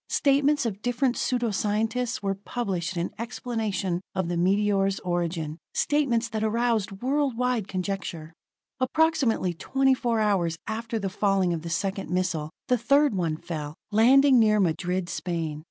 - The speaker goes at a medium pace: Yes, average, 145 wpm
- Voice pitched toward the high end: Yes, high, 205 Hz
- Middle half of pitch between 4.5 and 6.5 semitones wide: Yes, average, 5.3 semitones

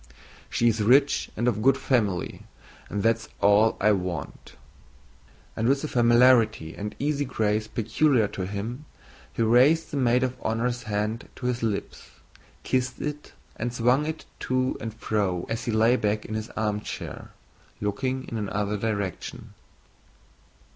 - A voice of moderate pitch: No, low, 115 Hz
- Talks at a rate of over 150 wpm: No, average, 145 wpm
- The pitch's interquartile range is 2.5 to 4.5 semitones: Yes, average, 3.3 semitones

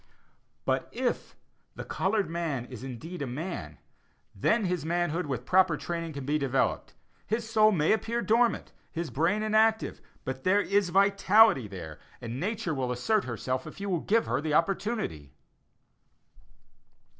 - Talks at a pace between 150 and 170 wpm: Yes, average, 155 wpm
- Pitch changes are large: Yes, wide, 7.6 semitones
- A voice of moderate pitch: Yes, medium, 170 Hz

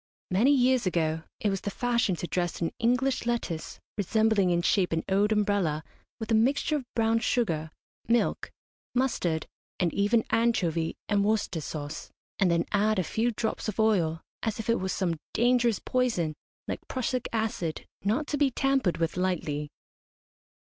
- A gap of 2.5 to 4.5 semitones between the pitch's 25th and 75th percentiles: No, wide, 5.4 semitones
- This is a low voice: No, high, 210 Hz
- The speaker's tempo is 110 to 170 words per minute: Yes, average, 160 wpm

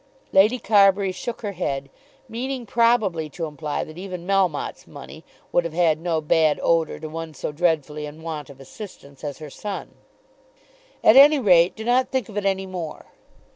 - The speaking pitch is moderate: Yes, medium, 175 Hz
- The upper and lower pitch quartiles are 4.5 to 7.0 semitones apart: Yes, average, 5.0 semitones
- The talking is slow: No, average, 175 wpm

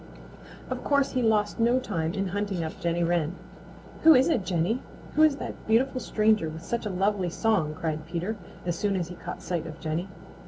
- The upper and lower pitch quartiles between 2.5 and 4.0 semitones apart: No, average, 5.1 semitones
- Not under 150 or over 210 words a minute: Yes, average, 200 wpm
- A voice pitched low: No, high, 195 Hz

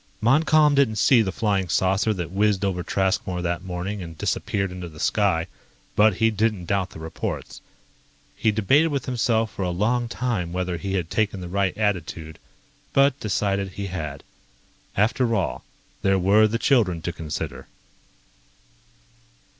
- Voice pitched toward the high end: No, low, 100 Hz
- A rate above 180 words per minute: No, average, 155 wpm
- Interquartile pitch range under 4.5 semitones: Yes, average, 3.7 semitones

